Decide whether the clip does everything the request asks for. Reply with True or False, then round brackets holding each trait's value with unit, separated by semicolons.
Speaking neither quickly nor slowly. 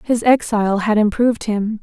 True (165 wpm)